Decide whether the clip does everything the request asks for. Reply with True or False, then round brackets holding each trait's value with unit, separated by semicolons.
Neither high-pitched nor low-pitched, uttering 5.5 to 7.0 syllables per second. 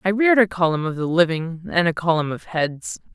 True (175 Hz; 5.7 syllables/s)